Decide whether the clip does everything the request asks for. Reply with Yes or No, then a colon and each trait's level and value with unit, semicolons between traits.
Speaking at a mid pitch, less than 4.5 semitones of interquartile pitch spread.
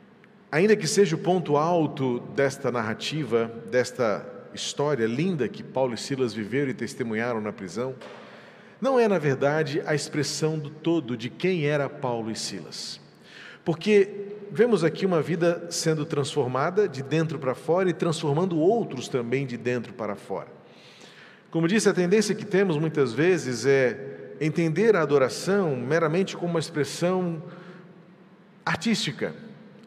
No: medium, 155 Hz; wide, 5.4 semitones